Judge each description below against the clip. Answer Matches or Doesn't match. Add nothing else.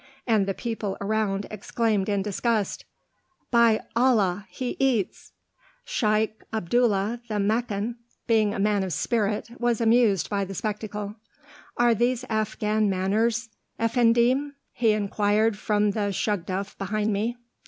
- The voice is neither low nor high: Doesn't match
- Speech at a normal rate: Doesn't match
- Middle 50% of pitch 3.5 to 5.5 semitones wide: Doesn't match